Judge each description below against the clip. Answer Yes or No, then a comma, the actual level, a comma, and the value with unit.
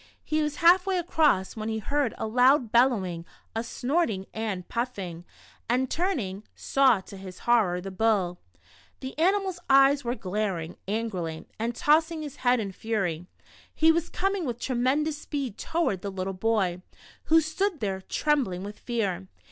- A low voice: No, high, 235 Hz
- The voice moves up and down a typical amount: No, wide, 7.4 semitones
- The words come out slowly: No, average, 155 wpm